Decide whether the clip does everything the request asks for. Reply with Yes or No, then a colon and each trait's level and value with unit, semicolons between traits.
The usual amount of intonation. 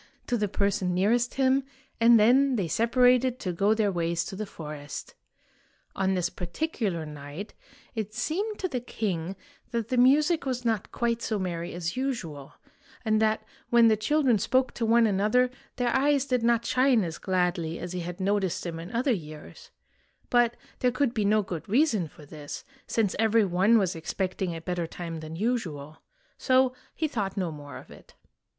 No: wide, 5.8 semitones